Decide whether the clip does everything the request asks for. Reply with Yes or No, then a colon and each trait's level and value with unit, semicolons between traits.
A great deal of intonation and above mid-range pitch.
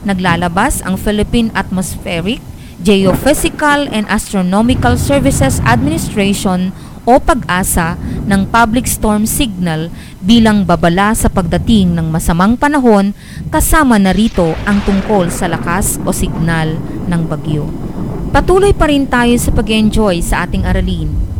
No: average, 4.9 semitones; high, 195 Hz